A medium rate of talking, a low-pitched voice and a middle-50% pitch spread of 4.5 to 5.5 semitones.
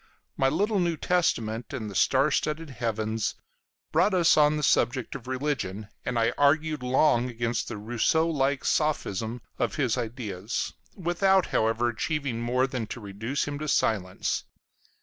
Yes: average, 150 wpm; low, 125 Hz; average, 5.1 semitones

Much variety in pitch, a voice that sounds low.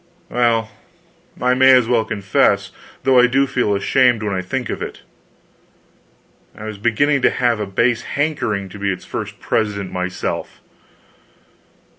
No: average, 3.9 semitones; low, 115 Hz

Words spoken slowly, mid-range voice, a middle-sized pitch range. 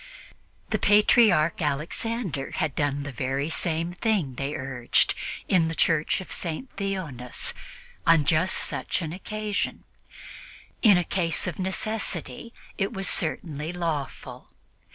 Yes: slow, 125 wpm; medium, 165 Hz; average, 5.0 semitones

